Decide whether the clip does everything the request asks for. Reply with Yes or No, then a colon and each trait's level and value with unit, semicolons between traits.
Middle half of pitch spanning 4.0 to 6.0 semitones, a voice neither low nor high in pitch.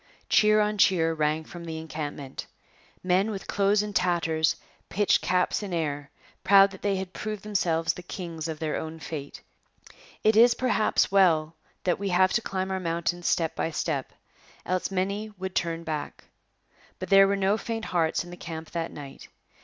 No: average, 3.5 semitones; medium, 180 Hz